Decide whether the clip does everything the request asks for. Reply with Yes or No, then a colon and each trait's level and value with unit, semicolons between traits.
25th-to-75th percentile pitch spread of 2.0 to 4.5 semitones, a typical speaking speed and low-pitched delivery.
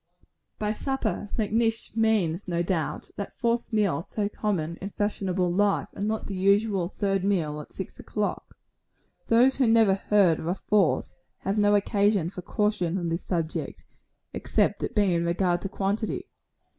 No: average, 3.2 semitones; average, 160 wpm; high, 200 Hz